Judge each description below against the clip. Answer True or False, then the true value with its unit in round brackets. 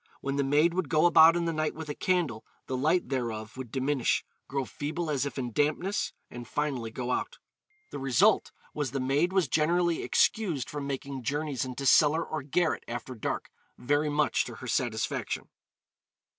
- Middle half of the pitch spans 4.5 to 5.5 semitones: False (3.5 semitones)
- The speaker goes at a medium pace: True (180 wpm)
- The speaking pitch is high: False (145 Hz)